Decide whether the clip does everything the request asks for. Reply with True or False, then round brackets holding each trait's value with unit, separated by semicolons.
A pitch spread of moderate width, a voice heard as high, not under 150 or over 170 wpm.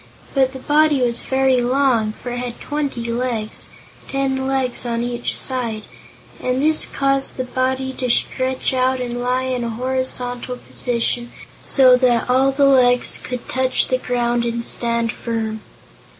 False (1.6 semitones; 250 Hz; 155 wpm)